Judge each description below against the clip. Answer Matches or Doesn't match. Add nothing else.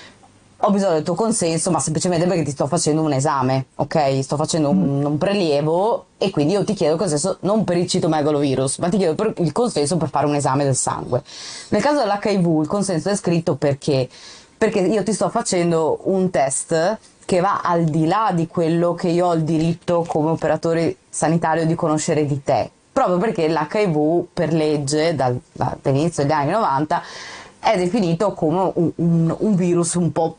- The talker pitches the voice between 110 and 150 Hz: Doesn't match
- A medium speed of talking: Doesn't match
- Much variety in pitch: Doesn't match